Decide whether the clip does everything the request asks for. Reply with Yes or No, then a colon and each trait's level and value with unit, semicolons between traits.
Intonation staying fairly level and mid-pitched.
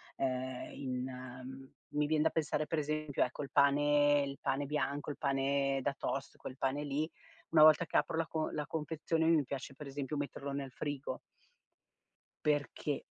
Yes: narrow, 1.8 semitones; medium, 145 Hz